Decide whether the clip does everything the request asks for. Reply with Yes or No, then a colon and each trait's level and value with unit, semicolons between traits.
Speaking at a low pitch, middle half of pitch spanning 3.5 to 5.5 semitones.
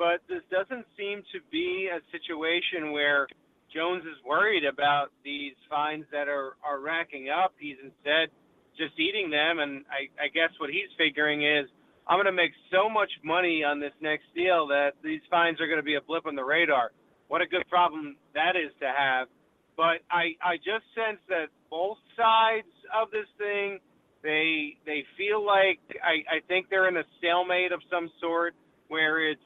No: medium, 165 Hz; average, 3.9 semitones